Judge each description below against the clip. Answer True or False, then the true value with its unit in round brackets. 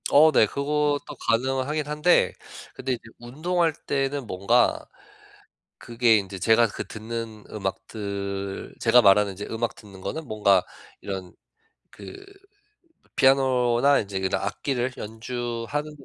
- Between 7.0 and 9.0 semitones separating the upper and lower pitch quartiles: False (5.3 semitones)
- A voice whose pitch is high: False (120 Hz)